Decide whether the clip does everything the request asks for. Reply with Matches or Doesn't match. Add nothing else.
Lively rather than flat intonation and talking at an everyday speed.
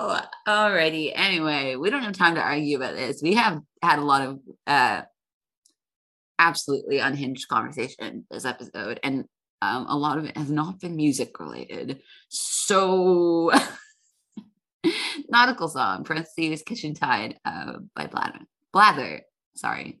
Doesn't match